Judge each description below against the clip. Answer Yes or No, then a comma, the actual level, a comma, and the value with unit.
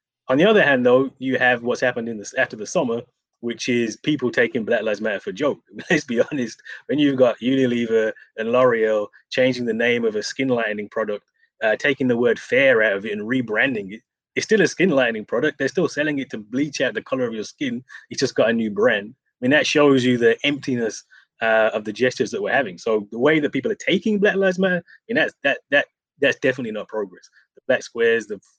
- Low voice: Yes, low, 130 Hz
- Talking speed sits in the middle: No, fast, 235 wpm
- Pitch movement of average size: No, wide, 8.1 semitones